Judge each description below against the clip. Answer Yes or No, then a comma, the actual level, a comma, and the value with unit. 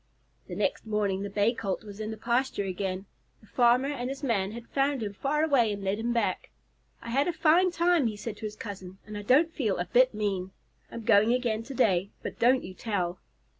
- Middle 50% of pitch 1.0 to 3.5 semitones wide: No, average, 4.3 semitones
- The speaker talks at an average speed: No, fast, 225 wpm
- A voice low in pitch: No, high, 225 Hz